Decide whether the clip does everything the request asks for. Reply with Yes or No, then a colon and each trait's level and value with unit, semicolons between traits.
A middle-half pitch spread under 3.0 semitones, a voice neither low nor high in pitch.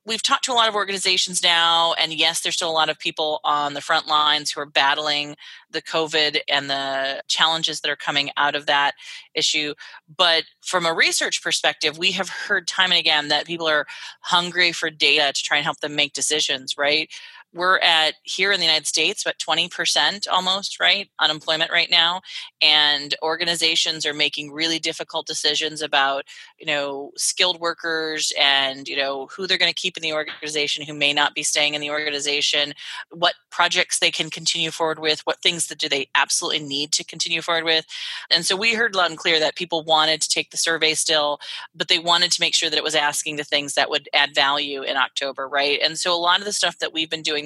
Yes: narrow, 2.5 semitones; medium, 160 Hz